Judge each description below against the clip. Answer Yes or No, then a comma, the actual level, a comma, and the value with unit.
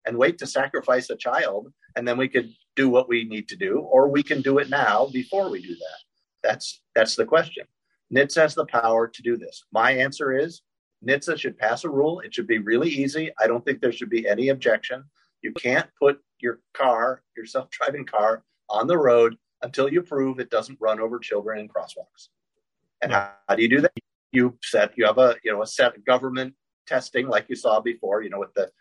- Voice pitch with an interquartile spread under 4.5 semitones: Yes, average, 3.5 semitones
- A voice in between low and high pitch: No, low, 130 Hz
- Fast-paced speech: Yes, fast, 220 wpm